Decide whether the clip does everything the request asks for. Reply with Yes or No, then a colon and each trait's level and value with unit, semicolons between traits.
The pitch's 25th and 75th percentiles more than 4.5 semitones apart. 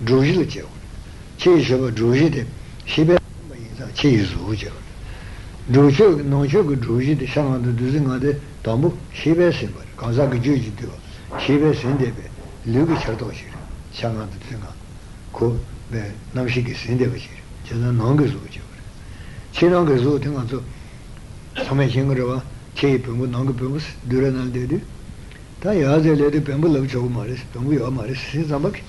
No: average, 3.9 semitones